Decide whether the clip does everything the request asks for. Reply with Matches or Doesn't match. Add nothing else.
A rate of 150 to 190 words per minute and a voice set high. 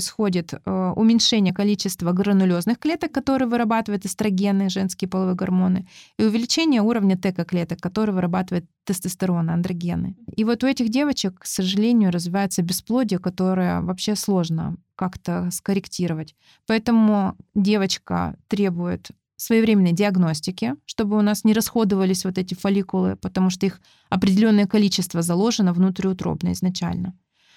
Doesn't match